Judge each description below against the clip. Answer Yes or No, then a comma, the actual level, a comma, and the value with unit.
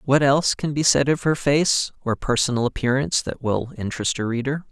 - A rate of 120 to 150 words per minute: No, fast, 205 wpm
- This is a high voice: No, low, 130 Hz